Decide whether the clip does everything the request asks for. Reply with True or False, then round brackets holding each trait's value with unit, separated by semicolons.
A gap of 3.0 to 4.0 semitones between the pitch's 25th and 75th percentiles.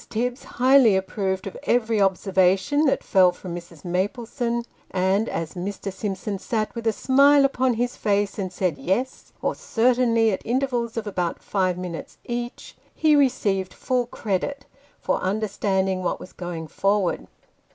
False (4.4 semitones)